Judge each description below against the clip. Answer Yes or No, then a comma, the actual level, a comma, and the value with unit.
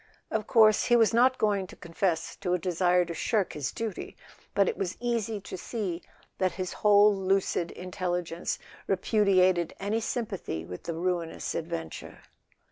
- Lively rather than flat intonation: No, average, 3.4 semitones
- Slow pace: No, average, 155 wpm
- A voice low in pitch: No, medium, 185 Hz